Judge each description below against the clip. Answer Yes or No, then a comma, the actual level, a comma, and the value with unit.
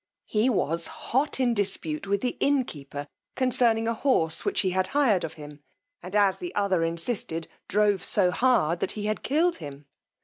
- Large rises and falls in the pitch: Yes, wide, 6.6 semitones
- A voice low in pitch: No, high, 200 Hz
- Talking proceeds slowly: No, average, 175 wpm